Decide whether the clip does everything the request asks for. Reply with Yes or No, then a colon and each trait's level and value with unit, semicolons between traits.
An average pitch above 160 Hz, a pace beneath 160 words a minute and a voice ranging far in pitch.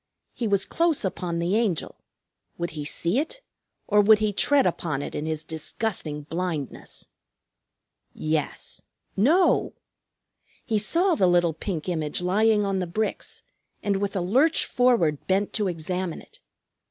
No: high, 190 Hz; average, 145 wpm; average, 4.7 semitones